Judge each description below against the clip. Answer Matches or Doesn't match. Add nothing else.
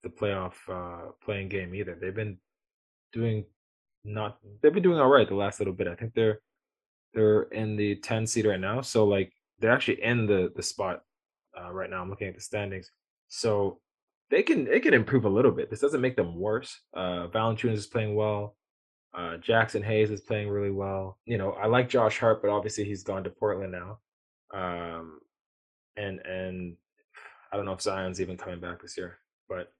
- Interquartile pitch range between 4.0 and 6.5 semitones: Doesn't match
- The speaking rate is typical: Matches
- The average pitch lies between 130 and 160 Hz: Doesn't match